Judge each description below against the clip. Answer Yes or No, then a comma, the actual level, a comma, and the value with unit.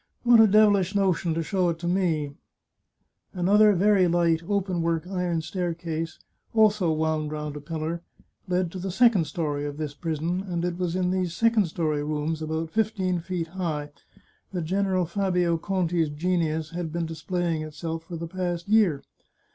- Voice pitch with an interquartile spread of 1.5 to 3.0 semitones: Yes, average, 2.7 semitones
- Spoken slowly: No, average, 175 wpm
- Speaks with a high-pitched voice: No, medium, 170 Hz